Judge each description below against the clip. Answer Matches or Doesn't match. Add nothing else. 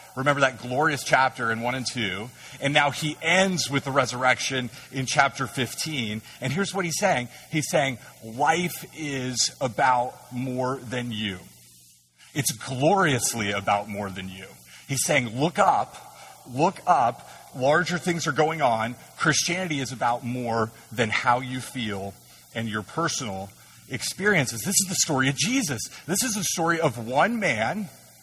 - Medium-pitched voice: Doesn't match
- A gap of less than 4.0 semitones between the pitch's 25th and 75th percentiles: Doesn't match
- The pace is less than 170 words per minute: Matches